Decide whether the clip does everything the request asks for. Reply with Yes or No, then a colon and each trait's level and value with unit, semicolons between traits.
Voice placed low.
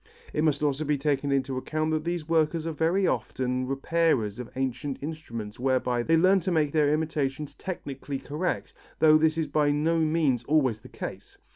No: medium, 150 Hz